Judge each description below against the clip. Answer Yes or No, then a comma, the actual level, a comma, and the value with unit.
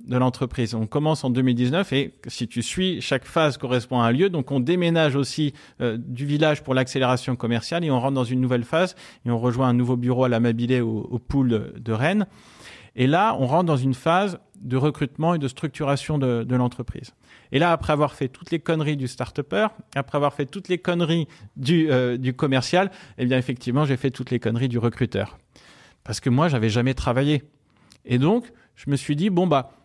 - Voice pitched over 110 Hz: Yes, low, 135 Hz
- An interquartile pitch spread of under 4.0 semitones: Yes, average, 3.6 semitones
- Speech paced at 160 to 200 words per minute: No, average, 215 wpm